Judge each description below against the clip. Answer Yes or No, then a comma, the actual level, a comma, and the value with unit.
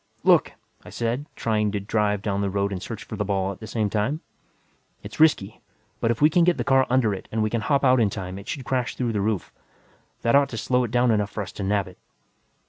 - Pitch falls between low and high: No, low, 110 Hz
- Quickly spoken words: Yes, fast, 255 wpm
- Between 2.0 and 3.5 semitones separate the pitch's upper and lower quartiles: No, average, 3.9 semitones